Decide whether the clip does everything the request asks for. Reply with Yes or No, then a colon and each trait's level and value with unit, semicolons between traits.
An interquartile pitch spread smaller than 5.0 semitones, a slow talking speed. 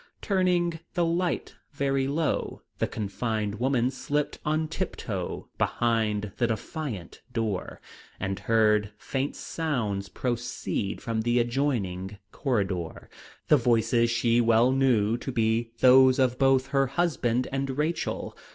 Yes: average, 3.8 semitones; slow, 125 wpm